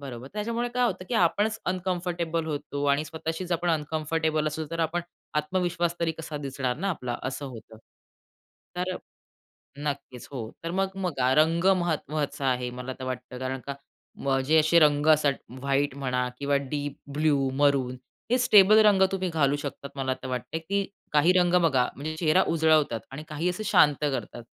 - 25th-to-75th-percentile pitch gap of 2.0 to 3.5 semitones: No, average, 3.9 semitones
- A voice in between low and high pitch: Yes, medium, 150 Hz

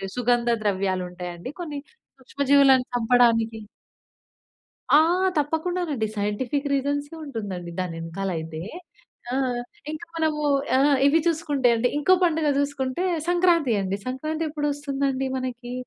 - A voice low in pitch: No, very high, 265 Hz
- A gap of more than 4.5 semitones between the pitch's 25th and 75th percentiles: Yes, average, 4.9 semitones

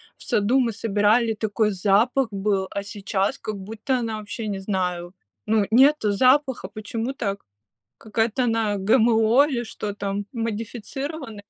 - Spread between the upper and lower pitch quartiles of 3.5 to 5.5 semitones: No, average, 2.7 semitones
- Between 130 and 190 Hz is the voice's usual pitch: No, high, 220 Hz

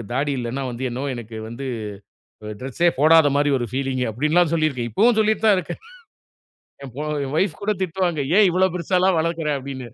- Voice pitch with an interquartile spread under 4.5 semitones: No, wide, 5.4 semitones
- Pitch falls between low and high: Yes, medium, 150 Hz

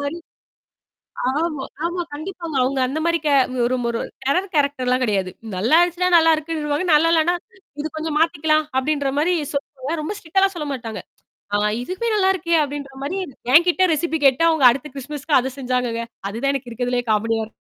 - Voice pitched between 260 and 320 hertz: Yes, very high, 295 Hz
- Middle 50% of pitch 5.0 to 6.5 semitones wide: No, average, 4.4 semitones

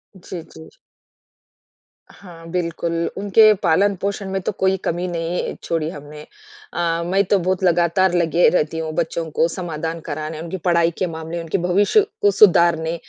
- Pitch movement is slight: Yes, narrow, 2.3 semitones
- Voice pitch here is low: No, medium, 170 Hz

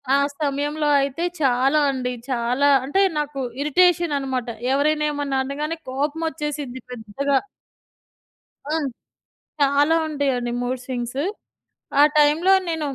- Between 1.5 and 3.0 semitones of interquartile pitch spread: Yes, narrow, 2.5 semitones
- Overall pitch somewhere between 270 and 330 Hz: Yes, very high, 285 Hz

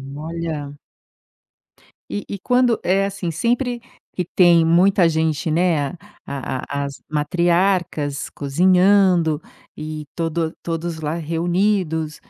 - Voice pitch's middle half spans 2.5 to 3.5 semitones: Yes, average, 3.1 semitones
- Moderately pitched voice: Yes, medium, 170 Hz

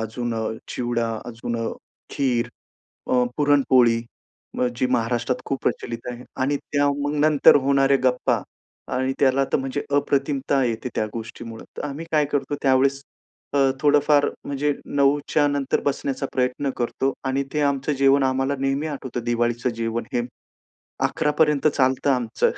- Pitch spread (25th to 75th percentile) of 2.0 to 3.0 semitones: Yes, average, 2.7 semitones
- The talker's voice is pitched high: No, low, 135 Hz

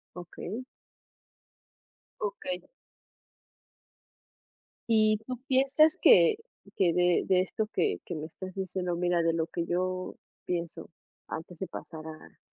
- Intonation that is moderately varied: Yes, average, 3.3 semitones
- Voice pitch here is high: No, medium, 180 Hz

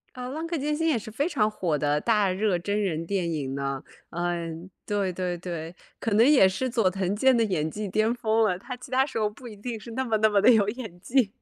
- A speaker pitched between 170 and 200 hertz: No, high, 210 Hz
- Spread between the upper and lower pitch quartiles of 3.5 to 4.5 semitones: No, average, 5.2 semitones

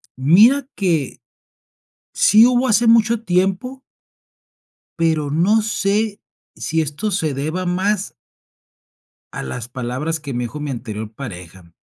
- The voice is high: No, medium, 165 Hz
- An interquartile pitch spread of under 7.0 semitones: No, wide, 7.7 semitones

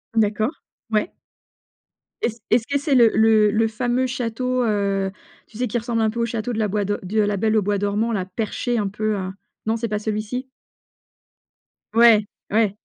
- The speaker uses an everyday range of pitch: No, narrow, 2.1 semitones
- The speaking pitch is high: Yes, high, 220 Hz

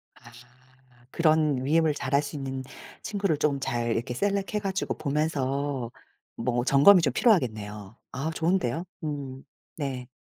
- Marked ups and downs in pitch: No, average, 4.0 semitones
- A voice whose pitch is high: No, medium, 140 Hz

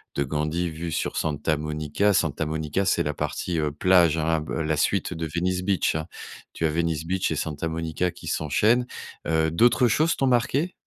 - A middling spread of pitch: Yes, average, 3.0 semitones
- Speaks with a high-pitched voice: No, very low, 80 Hz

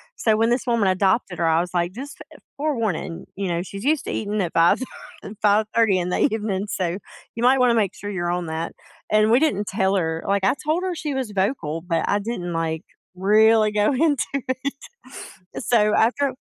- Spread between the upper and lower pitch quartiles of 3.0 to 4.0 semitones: No, average, 4.9 semitones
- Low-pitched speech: No, high, 210 Hz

